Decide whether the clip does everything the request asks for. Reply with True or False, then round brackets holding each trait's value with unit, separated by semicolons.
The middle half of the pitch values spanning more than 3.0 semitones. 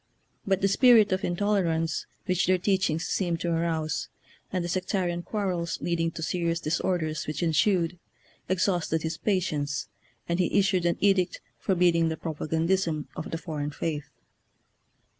False (2.5 semitones)